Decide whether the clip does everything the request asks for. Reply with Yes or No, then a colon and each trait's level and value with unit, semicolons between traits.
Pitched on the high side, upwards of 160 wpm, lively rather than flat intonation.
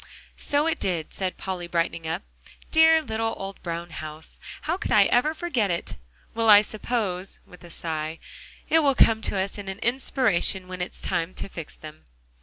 Yes: high, 195 Hz; average, 185 wpm; wide, 5.7 semitones